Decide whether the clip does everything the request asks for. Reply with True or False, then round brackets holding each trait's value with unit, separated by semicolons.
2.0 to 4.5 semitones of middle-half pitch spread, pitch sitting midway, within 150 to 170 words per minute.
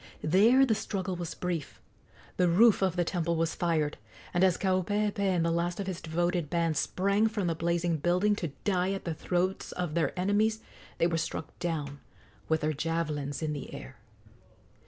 False (2.7 semitones; 175 Hz; 180 wpm)